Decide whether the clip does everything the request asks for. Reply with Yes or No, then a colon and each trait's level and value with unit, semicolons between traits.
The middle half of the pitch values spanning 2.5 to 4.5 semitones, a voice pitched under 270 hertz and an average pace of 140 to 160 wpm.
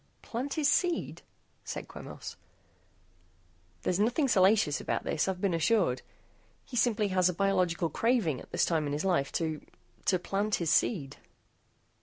No: wide, 5.5 semitones; medium, 185 Hz; average, 150 wpm